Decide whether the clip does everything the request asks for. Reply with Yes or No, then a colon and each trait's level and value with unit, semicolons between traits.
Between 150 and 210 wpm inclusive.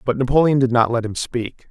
No: fast, 245 wpm